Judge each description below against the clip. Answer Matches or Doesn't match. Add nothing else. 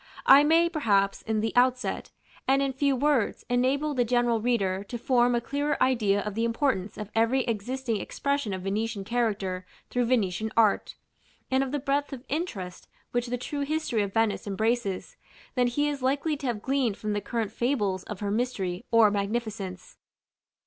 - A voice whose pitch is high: Matches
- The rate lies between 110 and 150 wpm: Doesn't match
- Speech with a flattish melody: Doesn't match